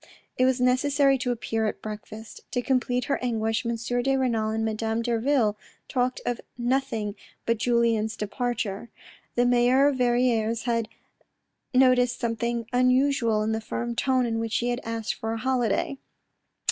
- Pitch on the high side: Yes, high, 240 Hz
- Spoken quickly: No, average, 155 wpm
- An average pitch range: No, narrow, 2.1 semitones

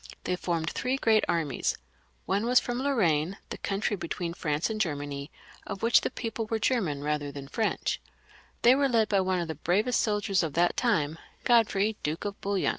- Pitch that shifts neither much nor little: No, wide, 5.9 semitones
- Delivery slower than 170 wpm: No, average, 190 wpm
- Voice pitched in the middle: No, high, 195 Hz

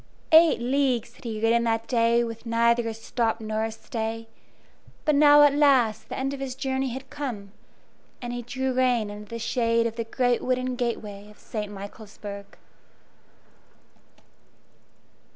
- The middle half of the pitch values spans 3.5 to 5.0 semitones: No, narrow, 2.5 semitones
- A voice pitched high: Yes, high, 235 Hz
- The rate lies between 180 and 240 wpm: No, average, 155 wpm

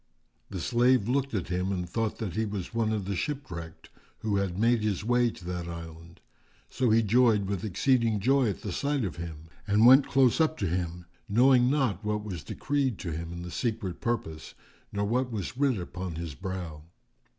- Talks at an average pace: Yes, average, 195 wpm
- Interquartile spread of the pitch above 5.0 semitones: Yes, wide, 5.5 semitones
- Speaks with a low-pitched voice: Yes, low, 105 Hz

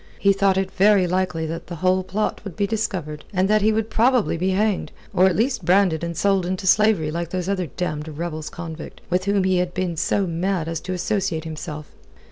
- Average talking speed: No, fast, 215 wpm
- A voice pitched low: No, medium, 185 Hz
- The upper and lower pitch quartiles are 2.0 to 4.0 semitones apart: Yes, average, 3.0 semitones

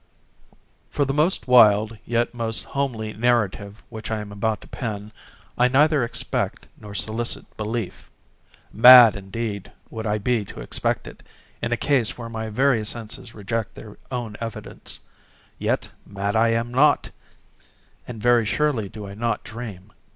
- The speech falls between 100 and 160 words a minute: Yes, average, 150 wpm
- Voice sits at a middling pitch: No, low, 115 Hz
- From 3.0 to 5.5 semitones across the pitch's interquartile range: No, narrow, 2.4 semitones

